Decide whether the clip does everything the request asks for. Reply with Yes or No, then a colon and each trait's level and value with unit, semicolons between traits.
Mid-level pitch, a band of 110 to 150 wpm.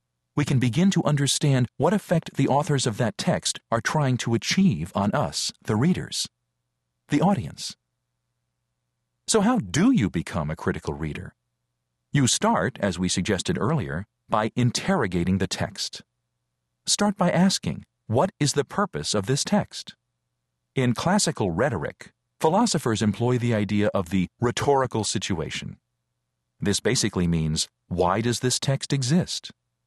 No: low, 105 Hz; average, 140 wpm